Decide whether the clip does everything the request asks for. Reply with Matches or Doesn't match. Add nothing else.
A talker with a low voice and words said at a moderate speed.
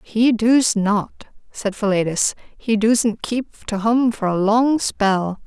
Doesn't match